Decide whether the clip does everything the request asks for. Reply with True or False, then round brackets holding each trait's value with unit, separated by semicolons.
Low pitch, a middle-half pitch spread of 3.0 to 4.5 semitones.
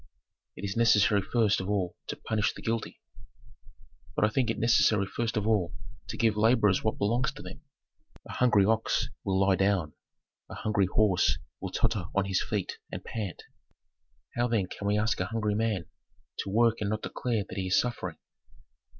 False (105 Hz; 2.5 semitones)